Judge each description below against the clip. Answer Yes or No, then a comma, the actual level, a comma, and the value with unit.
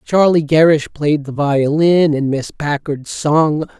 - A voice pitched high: No, medium, 150 Hz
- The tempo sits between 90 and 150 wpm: Yes, average, 140 wpm